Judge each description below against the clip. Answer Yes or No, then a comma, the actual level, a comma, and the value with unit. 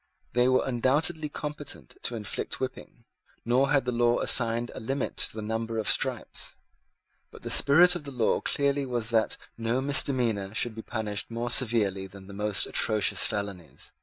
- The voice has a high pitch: No, low, 120 Hz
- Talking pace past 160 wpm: Yes, average, 170 wpm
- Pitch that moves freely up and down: No, average, 3.5 semitones